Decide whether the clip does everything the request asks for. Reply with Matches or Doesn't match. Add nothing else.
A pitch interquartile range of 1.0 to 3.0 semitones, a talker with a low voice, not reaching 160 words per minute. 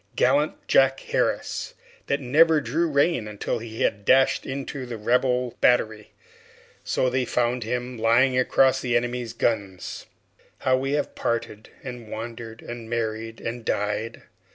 Matches